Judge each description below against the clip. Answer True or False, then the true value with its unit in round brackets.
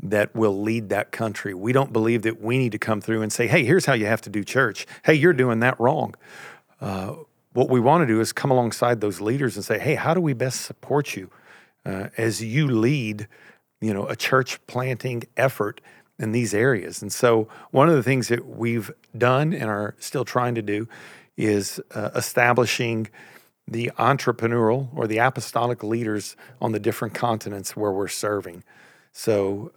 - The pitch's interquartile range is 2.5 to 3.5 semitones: True (2.9 semitones)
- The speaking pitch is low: True (115 Hz)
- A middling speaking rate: True (190 wpm)